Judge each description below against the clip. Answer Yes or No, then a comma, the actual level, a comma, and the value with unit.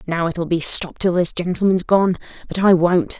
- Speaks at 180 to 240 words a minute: Yes, fast, 205 wpm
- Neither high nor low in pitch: Yes, medium, 175 Hz